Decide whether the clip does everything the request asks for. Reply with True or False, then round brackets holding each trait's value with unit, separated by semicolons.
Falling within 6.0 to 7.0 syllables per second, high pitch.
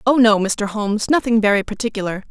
True (6.1 syllables/s; 215 Hz)